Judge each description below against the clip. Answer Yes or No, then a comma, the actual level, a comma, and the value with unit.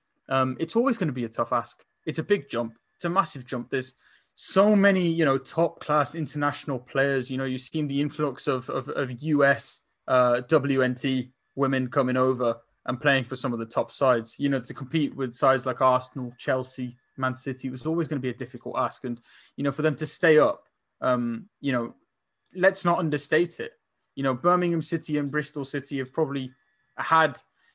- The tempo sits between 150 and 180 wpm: No, fast, 205 wpm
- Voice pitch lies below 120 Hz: No, low, 135 Hz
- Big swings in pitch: No, average, 3.3 semitones